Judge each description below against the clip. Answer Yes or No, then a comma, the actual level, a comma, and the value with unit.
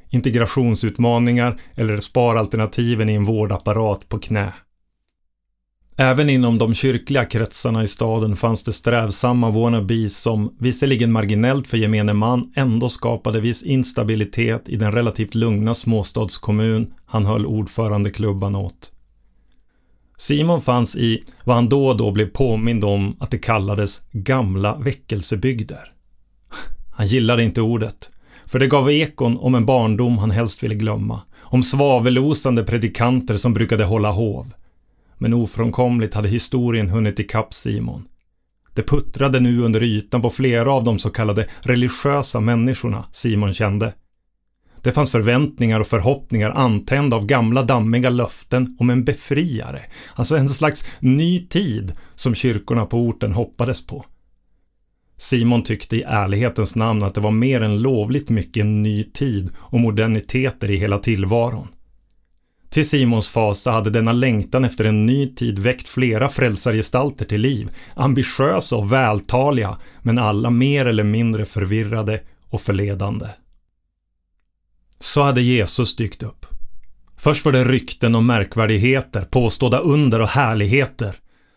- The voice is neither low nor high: No, low, 115 Hz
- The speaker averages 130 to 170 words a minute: Yes, average, 135 wpm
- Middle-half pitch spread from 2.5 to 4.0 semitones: Yes, average, 3.0 semitones